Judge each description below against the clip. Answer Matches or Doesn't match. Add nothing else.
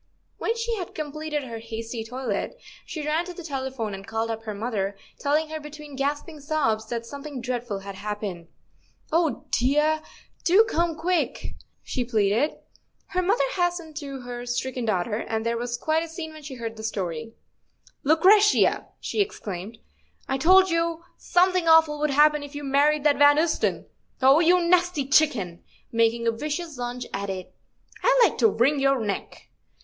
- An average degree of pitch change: Doesn't match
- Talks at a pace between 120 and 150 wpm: Doesn't match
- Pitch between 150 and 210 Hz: Doesn't match